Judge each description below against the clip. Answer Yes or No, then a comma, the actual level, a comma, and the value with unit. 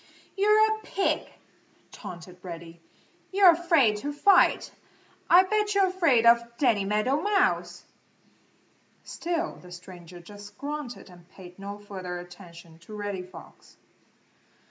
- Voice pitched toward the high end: Yes, high, 210 Hz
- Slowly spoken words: Yes, slow, 120 wpm